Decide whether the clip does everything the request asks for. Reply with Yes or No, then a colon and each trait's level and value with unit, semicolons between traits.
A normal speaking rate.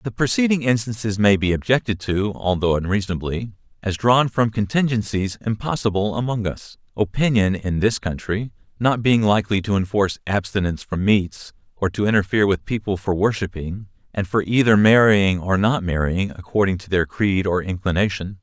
Yes: average, 155 wpm